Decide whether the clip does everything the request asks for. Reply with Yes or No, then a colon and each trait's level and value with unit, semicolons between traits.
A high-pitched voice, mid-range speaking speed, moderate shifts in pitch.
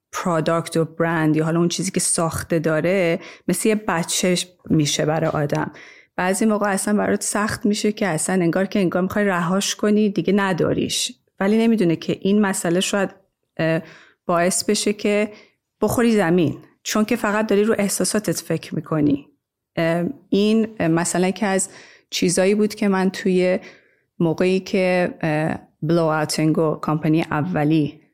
No: medium, 180 Hz; average, 145 wpm; average, 3.9 semitones